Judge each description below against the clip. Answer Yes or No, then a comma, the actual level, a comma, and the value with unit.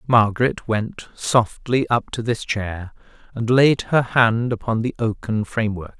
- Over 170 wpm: No, average, 150 wpm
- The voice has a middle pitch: No, low, 115 Hz